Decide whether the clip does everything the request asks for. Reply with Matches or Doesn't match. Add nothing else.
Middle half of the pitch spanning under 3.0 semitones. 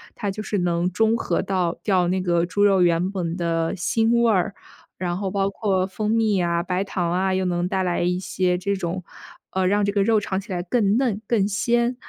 Matches